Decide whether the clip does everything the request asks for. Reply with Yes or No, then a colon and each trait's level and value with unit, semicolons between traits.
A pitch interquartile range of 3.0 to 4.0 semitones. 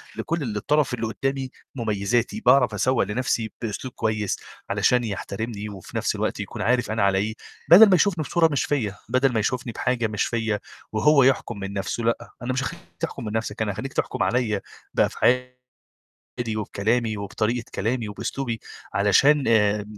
Yes: average, 3.5 semitones